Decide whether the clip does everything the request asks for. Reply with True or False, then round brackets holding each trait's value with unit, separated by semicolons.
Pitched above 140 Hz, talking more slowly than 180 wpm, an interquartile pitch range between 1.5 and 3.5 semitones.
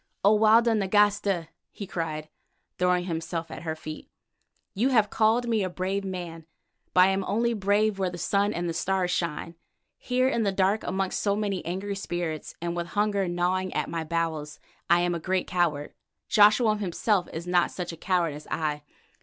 False (185 Hz; 185 wpm; 3.2 semitones)